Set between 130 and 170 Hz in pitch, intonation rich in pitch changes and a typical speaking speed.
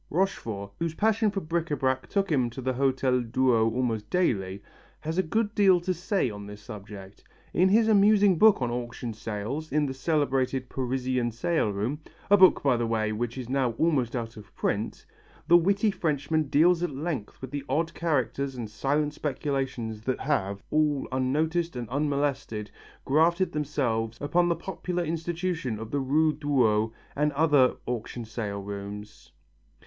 Yes: low, 135 Hz; wide, 5.9 semitones; average, 165 wpm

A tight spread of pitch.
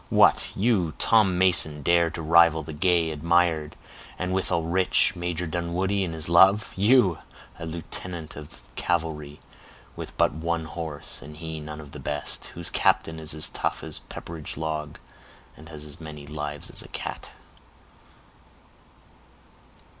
Yes: narrow, 2.3 semitones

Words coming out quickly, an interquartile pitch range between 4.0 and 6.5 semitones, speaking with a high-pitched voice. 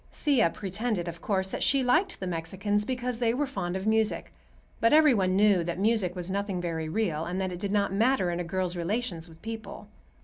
Yes: fast, 215 wpm; average, 4.3 semitones; high, 195 Hz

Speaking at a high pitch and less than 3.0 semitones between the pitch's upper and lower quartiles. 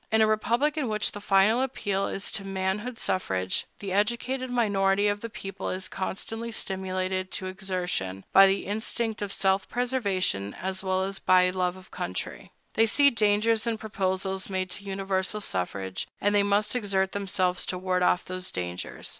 Yes: high, 195 Hz; narrow, 2.4 semitones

